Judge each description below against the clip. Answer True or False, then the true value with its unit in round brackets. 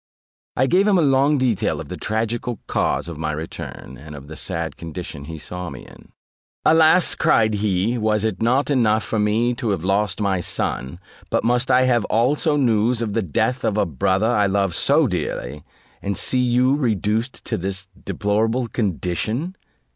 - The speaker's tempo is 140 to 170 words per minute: False (180 wpm)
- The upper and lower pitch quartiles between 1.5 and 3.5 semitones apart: False (5.1 semitones)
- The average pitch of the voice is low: True (110 Hz)